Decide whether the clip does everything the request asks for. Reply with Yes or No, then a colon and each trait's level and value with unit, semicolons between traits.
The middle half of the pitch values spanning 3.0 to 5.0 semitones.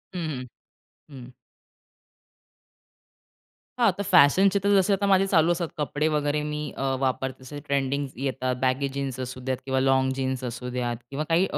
Yes: average, 3.6 semitones